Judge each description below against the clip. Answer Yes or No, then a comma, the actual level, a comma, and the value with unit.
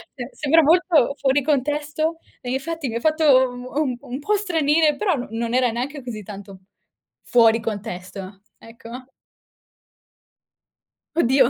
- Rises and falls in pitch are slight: No, average, 4.5 semitones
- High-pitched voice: Yes, very high, 260 Hz